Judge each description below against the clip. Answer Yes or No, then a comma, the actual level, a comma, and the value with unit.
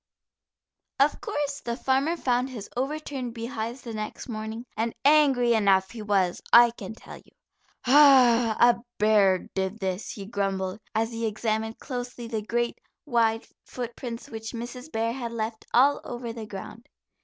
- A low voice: No, high, 230 Hz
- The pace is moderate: Yes, average, 155 wpm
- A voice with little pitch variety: Yes, narrow, 2.3 semitones